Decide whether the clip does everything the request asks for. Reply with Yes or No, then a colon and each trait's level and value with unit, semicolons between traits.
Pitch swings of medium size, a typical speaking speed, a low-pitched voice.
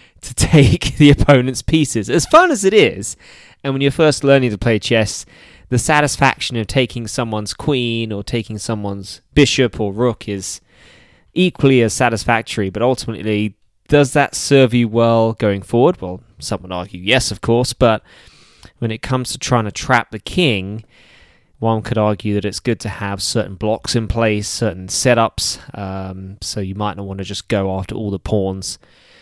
Yes: average, 4.0 semitones; average, 180 wpm; low, 115 Hz